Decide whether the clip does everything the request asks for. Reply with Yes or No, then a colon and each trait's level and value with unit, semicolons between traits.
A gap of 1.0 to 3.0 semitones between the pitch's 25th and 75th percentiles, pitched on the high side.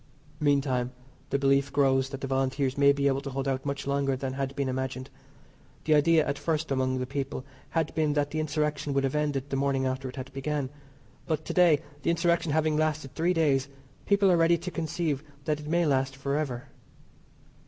No: narrow, 2.4 semitones; medium, 140 Hz